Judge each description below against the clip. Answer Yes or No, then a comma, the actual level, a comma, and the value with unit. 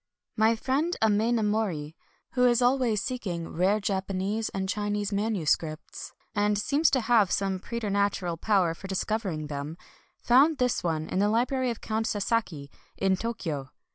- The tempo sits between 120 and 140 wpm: No, average, 150 wpm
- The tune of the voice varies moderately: Yes, average, 3.8 semitones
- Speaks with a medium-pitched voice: No, high, 205 Hz